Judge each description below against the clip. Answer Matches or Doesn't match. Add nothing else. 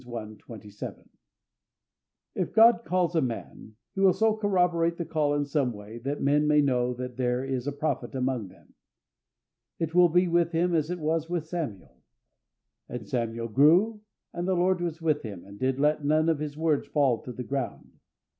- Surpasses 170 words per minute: Matches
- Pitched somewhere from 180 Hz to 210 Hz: Doesn't match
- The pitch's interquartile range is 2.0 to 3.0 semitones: Doesn't match